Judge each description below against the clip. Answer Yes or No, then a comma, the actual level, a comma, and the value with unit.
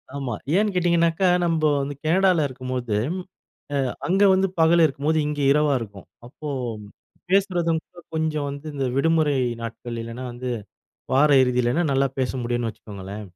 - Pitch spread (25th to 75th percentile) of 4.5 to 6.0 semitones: Yes, average, 5.2 semitones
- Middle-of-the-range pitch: Yes, medium, 145 Hz